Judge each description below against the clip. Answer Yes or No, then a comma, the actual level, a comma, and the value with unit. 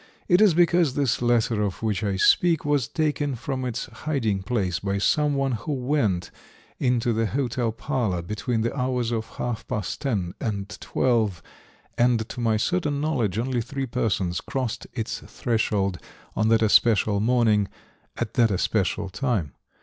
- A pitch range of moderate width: Yes, average, 4.1 semitones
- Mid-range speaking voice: No, low, 115 Hz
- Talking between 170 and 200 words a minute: No, average, 155 wpm